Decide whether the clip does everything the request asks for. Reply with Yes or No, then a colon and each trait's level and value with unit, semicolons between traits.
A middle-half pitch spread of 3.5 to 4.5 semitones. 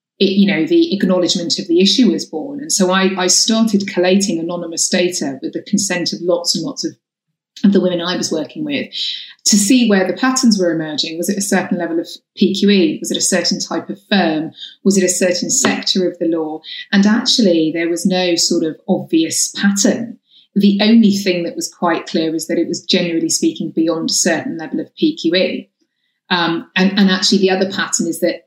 No: average, 3.0 semitones